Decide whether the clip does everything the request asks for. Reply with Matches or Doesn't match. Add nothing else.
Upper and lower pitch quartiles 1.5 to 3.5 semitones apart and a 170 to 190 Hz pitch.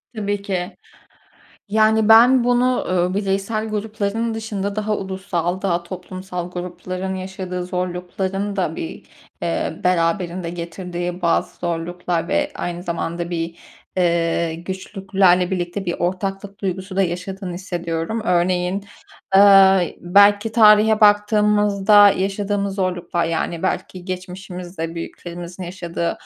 Matches